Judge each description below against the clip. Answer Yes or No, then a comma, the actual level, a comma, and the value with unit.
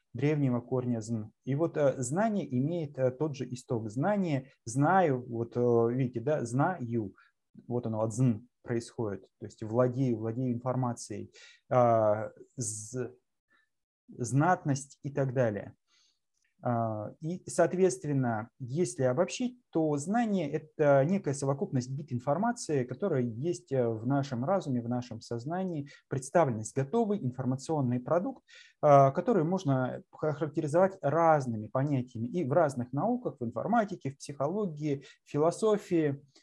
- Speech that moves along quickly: No, average, 120 wpm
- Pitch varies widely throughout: No, average, 5.0 semitones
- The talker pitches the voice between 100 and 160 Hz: Yes, low, 135 Hz